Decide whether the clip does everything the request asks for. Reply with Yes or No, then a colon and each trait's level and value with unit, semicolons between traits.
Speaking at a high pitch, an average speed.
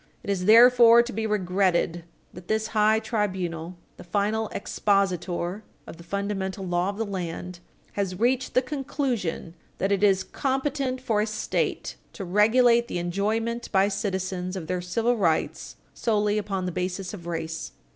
Yes: high, 200 Hz; average, 155 wpm